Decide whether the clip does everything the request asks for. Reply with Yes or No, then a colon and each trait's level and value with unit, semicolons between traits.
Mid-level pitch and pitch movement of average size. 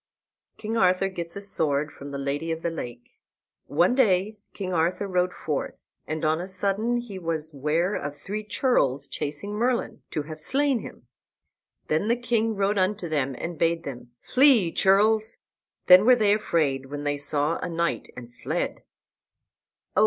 No: medium, 175 Hz; wide, 5.7 semitones